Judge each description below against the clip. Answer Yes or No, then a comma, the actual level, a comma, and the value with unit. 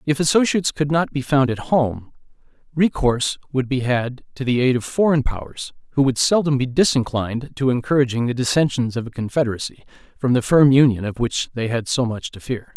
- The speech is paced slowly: No, average, 195 wpm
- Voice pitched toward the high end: No, low, 130 Hz